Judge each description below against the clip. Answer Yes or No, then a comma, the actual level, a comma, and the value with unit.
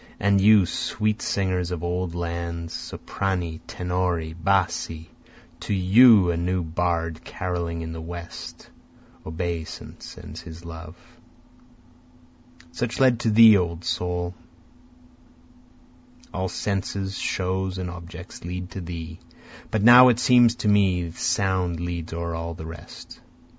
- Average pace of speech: No, slow, 125 wpm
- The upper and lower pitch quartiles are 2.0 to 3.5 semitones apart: Yes, narrow, 2.4 semitones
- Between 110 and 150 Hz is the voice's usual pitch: No, very low, 90 Hz